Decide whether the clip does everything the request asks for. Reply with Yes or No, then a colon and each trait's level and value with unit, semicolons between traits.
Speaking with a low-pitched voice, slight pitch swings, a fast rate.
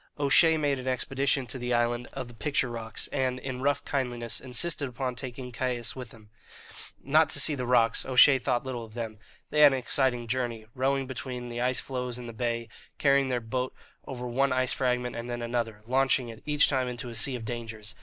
Yes: low, 125 Hz; narrow, 2.1 semitones; fast, 210 wpm